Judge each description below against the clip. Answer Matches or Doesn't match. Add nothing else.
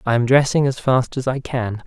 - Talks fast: Matches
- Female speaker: Doesn't match